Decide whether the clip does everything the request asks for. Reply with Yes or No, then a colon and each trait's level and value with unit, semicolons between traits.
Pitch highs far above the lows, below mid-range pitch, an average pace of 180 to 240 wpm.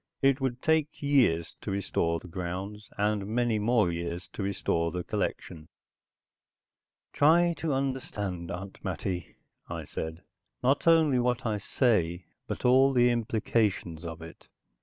No: wide, 6.6 semitones; low, 105 Hz; average, 140 wpm